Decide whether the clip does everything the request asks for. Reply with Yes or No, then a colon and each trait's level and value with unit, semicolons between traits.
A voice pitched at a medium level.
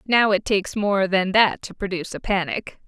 No: high, 195 Hz